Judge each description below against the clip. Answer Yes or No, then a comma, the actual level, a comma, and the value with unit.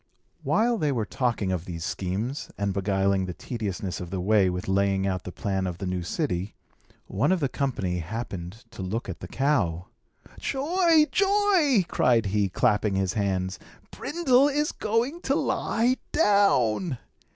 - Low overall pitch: Yes, low, 105 Hz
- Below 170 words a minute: Yes, average, 160 wpm